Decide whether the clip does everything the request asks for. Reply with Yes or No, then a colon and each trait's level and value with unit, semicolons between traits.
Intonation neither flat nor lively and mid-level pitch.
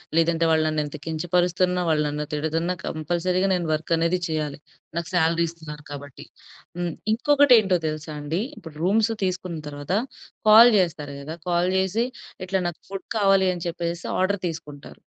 Yes: average, 3.0 semitones; medium, 170 Hz